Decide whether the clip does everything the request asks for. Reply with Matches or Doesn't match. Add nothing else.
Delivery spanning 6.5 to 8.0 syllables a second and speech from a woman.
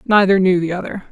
Doesn't match